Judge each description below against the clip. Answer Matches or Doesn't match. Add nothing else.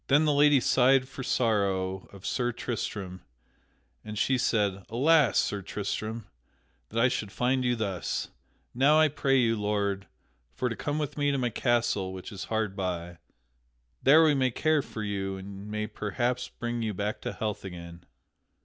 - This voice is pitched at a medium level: Doesn't match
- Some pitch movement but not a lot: Matches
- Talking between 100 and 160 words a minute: Doesn't match